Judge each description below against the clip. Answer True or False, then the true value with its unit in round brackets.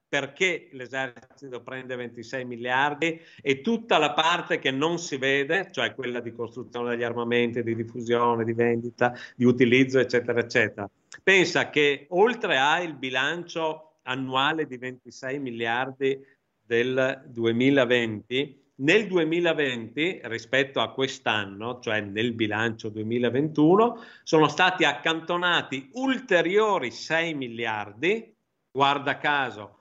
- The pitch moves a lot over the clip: False (4.1 semitones)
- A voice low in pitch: True (130 Hz)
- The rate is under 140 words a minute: True (115 wpm)